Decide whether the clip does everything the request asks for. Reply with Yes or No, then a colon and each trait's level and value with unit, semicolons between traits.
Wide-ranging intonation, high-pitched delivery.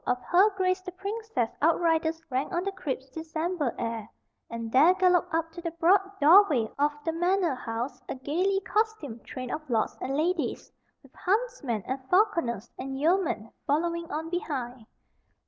Yes: wide, 5.8 semitones; very high, 325 Hz